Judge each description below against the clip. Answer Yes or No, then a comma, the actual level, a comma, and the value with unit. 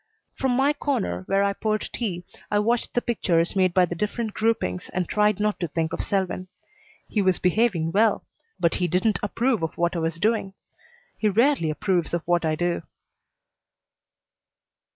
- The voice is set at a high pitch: Yes, high, 195 Hz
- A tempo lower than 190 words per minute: Yes, average, 175 wpm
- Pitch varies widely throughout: No, average, 4.2 semitones